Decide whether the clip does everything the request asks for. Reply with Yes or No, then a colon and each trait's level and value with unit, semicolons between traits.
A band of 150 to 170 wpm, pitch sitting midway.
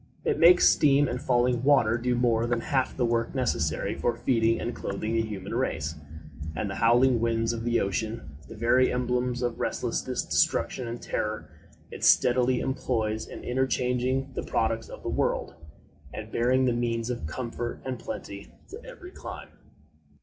No: average, 165 wpm; low, 120 Hz